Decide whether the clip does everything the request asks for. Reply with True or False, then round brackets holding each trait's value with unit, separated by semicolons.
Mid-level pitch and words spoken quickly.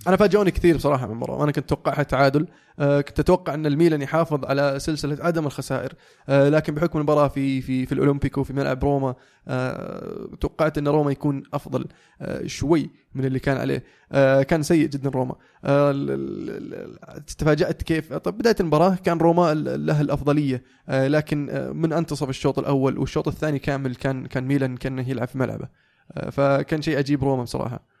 True (145 Hz; 155 wpm)